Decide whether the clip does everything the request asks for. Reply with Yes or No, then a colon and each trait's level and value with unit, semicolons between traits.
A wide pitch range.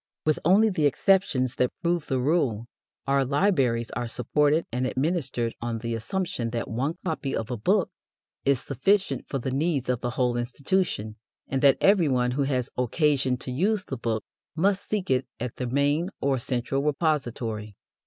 No: average, 4.6 semitones